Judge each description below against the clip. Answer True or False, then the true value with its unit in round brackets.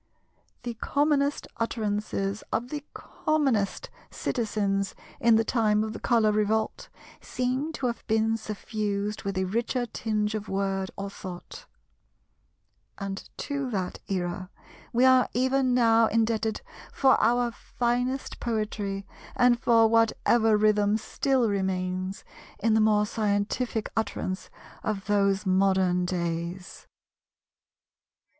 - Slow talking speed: True (115 wpm)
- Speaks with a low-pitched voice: False (215 Hz)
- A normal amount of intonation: True (3.2 semitones)